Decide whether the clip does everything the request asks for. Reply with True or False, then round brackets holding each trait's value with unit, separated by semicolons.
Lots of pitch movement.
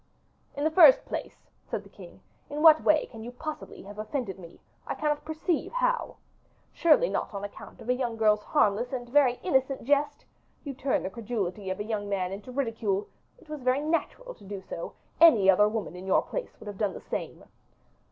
True (6.7 semitones)